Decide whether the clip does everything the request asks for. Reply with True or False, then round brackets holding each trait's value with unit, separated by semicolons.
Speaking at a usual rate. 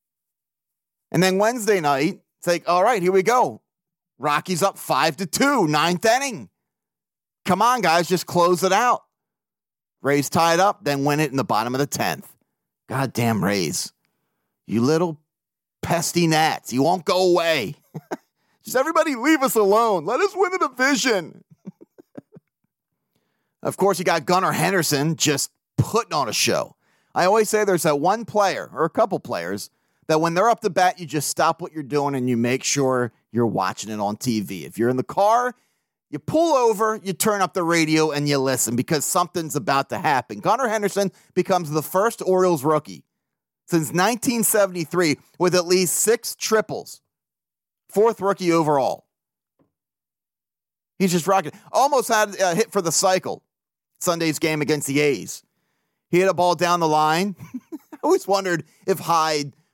True (165 wpm)